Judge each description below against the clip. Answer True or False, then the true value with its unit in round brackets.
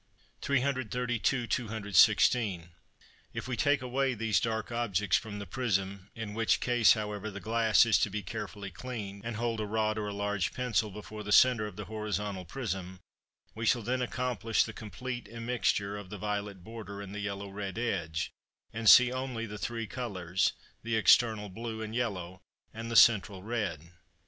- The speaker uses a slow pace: False (170 wpm)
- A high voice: False (110 Hz)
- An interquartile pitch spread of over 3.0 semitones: False (2.7 semitones)